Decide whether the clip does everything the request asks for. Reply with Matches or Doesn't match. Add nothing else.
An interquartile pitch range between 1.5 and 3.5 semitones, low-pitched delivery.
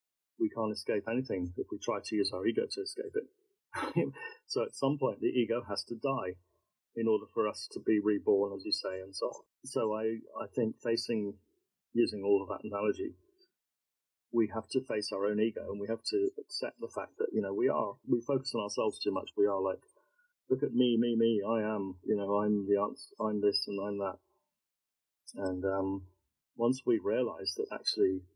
Doesn't match